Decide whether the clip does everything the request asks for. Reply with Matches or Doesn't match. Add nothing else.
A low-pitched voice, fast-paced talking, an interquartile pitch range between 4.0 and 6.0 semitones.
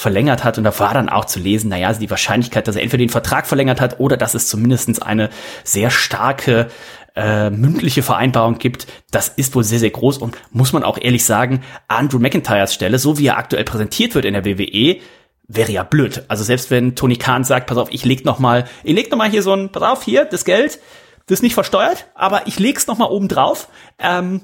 Matches